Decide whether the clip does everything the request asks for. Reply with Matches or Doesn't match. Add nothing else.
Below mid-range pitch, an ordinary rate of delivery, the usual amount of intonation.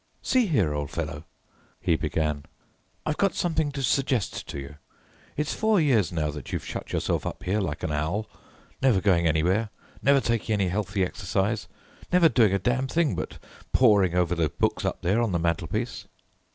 Doesn't match